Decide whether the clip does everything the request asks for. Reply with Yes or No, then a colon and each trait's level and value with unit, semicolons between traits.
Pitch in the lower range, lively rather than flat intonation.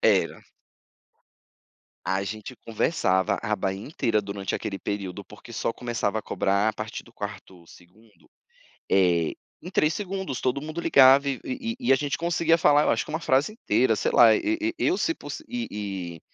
Yes: low, 120 Hz; wide, 8.9 semitones